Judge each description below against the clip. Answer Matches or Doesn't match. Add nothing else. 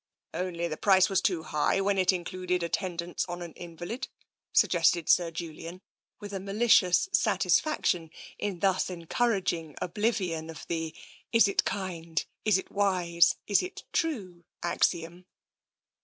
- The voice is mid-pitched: Matches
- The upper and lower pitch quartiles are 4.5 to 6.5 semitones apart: Doesn't match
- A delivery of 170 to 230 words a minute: Doesn't match